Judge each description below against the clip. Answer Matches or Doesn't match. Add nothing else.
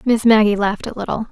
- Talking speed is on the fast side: Matches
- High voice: Matches